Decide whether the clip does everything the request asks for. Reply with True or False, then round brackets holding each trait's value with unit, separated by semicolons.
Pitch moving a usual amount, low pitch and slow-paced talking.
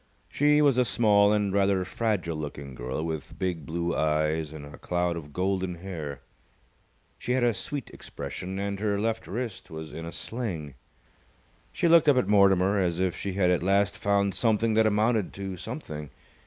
False (4.7 semitones; 95 Hz; 180 wpm)